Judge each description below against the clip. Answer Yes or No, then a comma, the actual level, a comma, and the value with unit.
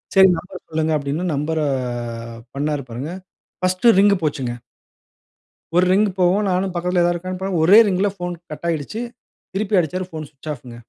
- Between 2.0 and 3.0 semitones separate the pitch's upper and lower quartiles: No, average, 3.6 semitones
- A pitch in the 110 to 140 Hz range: No, medium, 175 Hz